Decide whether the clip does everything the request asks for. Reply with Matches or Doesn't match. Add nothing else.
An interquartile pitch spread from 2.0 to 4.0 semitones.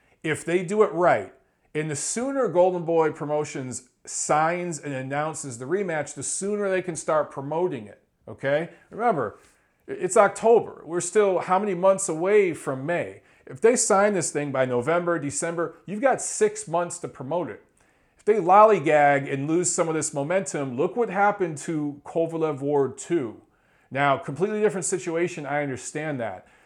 Doesn't match